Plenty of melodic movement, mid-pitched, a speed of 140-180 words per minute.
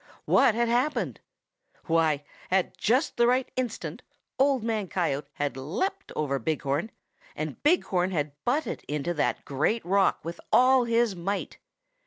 No: wide, 8.0 semitones; high, 195 Hz; average, 150 wpm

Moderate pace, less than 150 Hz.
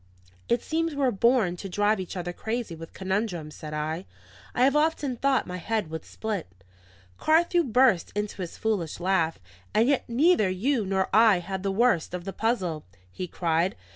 No: average, 180 wpm; high, 200 Hz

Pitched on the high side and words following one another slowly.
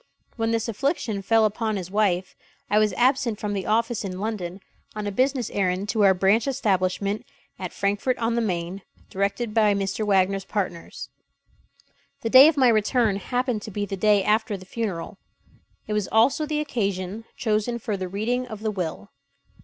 No: high, 210 Hz; average, 175 wpm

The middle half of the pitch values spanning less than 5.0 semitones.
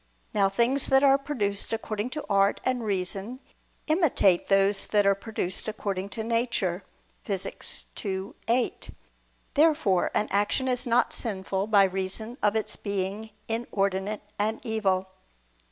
Yes: average, 3.3 semitones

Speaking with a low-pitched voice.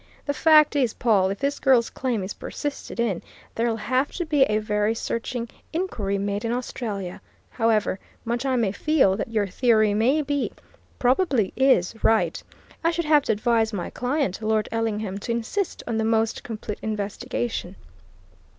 No: high, 230 Hz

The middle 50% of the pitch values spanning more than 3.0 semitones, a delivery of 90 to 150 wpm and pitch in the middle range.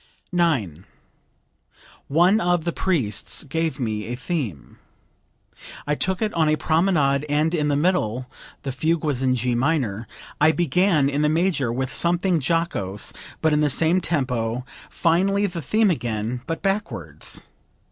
Yes: wide, 5.4 semitones; average, 145 wpm; medium, 150 Hz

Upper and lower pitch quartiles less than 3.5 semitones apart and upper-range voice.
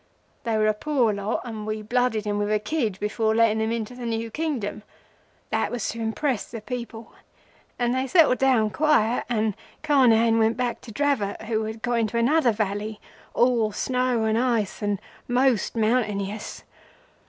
Yes: narrow, 2.6 semitones; high, 225 Hz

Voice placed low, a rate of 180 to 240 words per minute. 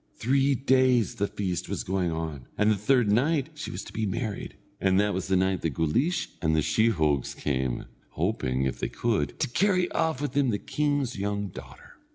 Yes: low, 105 Hz; average, 200 wpm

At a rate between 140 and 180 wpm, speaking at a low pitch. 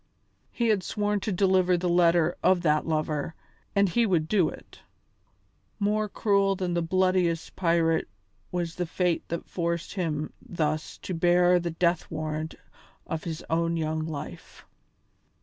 No: average, 150 wpm; medium, 170 Hz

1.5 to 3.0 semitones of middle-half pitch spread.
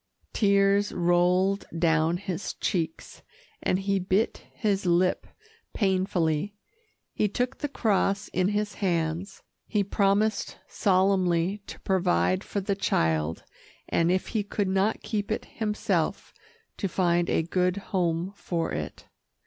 Yes: narrow, 2.5 semitones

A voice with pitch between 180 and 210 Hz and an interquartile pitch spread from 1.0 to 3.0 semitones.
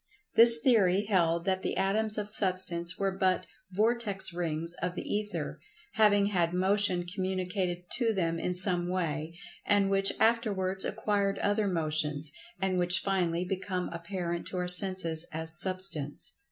Yes: medium, 185 Hz; narrow, 2.6 semitones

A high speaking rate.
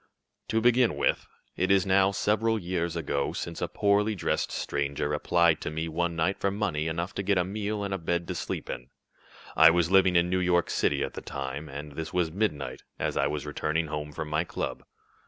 Yes: fast, 210 wpm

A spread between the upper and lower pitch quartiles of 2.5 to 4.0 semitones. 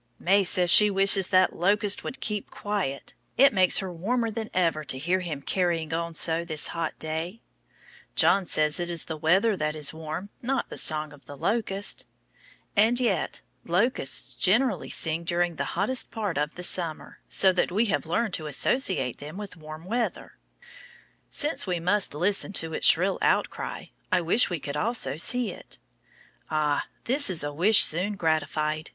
No: average, 4.6 semitones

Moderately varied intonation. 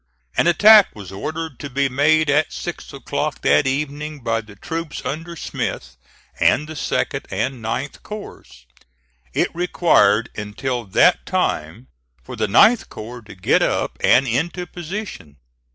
No: wide, 7.1 semitones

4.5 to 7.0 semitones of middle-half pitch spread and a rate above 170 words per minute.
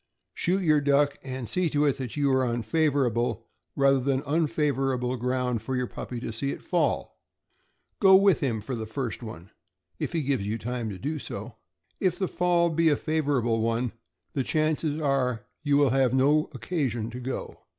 No: average, 3.8 semitones; average, 185 wpm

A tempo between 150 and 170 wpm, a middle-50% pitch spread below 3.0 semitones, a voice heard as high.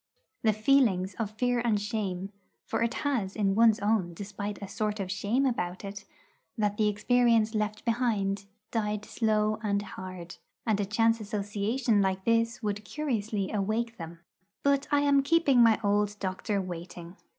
Yes: average, 160 wpm; narrow, 2.6 semitones; high, 210 Hz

